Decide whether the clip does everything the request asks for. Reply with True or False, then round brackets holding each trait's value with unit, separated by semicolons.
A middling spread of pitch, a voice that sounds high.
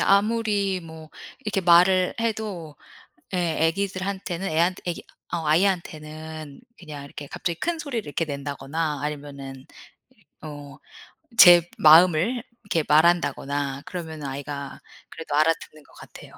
False (4.0 semitones; 165 Hz)